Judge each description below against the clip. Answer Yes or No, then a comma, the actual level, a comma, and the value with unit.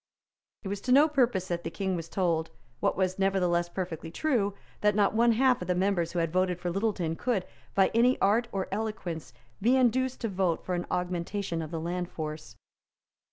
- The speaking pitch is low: No, high, 190 Hz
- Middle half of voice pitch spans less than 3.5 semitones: No, average, 4.1 semitones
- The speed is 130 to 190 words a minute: No, average, 200 wpm